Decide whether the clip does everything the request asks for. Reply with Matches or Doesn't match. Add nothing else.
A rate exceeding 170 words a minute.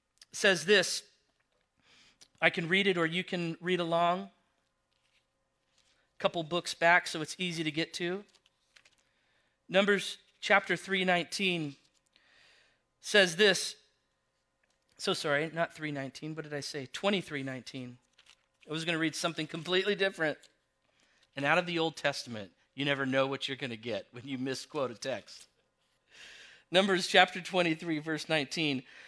Doesn't match